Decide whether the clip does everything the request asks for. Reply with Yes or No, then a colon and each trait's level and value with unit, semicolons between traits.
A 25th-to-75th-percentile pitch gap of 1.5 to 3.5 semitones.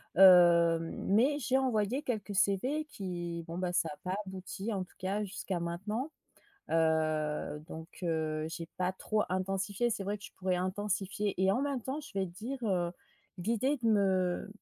No: average, 3.9 semitones